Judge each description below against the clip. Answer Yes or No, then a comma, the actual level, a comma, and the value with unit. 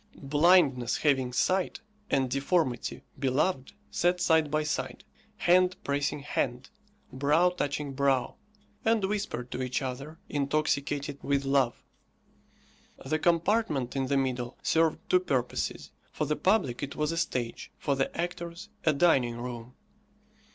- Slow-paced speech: Yes, slow, 130 wpm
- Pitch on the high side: No, medium, 140 Hz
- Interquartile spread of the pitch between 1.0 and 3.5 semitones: No, average, 4.3 semitones